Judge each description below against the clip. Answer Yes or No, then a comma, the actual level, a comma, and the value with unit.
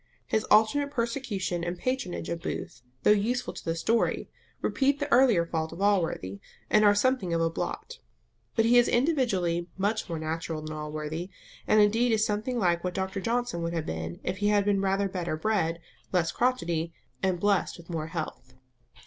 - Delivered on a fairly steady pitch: No, average, 5.1 semitones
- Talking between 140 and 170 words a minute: No, average, 185 wpm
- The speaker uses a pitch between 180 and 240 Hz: Yes, high, 190 Hz